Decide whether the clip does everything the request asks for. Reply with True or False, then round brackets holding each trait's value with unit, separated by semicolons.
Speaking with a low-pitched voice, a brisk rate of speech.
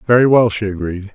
True (105 Hz; 210 wpm)